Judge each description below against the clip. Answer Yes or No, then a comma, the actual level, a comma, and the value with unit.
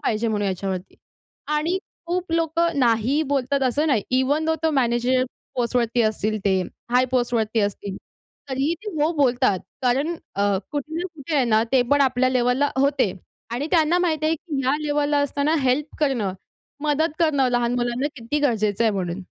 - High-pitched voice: Yes, very high, 260 Hz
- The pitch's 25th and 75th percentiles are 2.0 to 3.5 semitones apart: No, average, 4.3 semitones